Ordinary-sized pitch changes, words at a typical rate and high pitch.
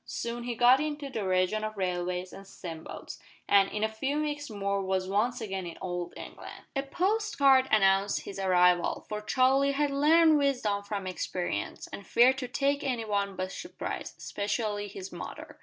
No: wide, 5.9 semitones; average, 180 wpm; high, 215 Hz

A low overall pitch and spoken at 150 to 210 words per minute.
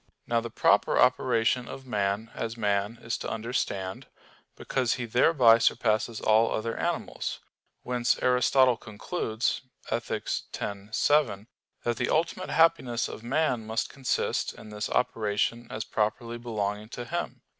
No: low, 115 Hz; slow, 135 wpm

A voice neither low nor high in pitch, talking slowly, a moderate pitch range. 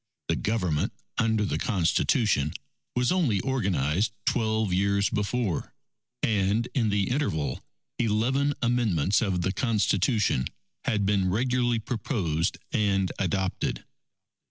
No: low, 105 Hz; slow, 110 wpm; average, 4.0 semitones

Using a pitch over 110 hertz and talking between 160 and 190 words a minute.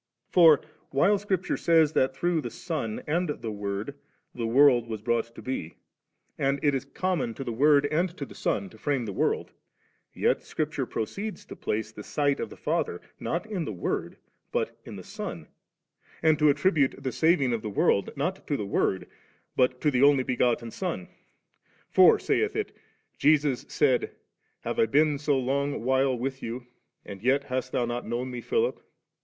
Yes: low, 135 Hz; average, 185 wpm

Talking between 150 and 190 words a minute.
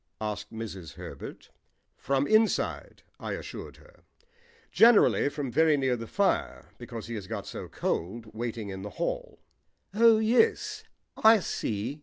No: average, 140 wpm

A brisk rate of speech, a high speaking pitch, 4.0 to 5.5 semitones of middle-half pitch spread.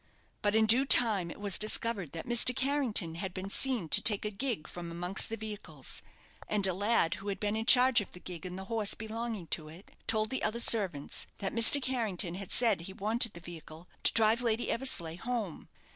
Yes: fast, 210 wpm; high, 210 Hz; average, 4.3 semitones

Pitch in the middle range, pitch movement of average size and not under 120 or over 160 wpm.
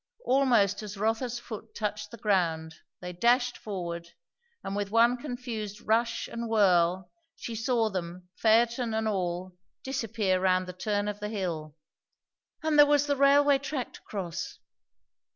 No: high, 215 Hz; average, 4.5 semitones; average, 150 wpm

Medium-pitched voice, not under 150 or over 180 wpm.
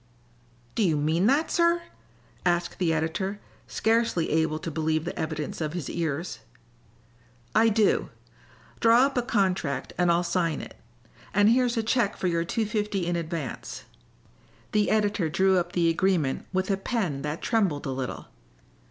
Yes: medium, 180 Hz; average, 160 wpm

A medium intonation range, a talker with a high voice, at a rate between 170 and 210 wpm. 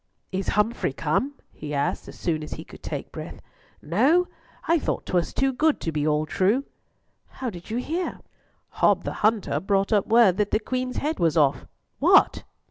No: wide, 7.7 semitones; high, 210 Hz; average, 185 wpm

